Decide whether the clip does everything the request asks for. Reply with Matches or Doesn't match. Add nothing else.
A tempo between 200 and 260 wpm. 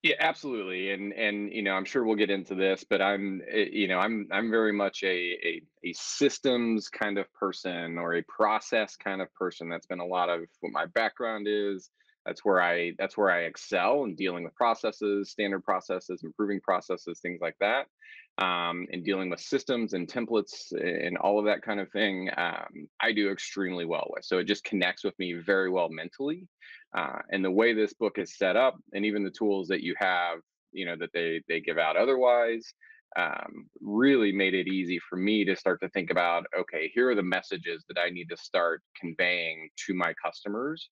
Matches